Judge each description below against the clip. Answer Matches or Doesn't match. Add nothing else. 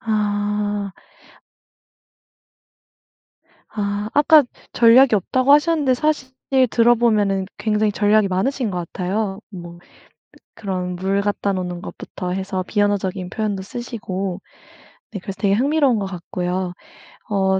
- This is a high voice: Matches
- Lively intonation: Doesn't match